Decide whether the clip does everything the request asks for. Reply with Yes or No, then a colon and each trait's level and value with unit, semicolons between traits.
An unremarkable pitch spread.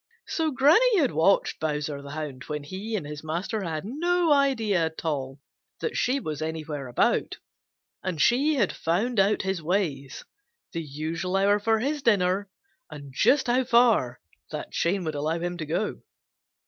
No: wide, 7.5 semitones